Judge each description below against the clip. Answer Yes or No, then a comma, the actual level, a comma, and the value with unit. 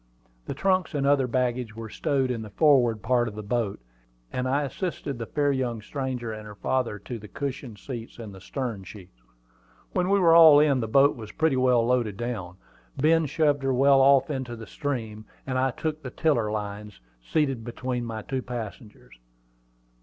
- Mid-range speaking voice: No, low, 125 Hz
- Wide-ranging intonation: No, average, 4.0 semitones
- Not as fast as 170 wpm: No, average, 190 wpm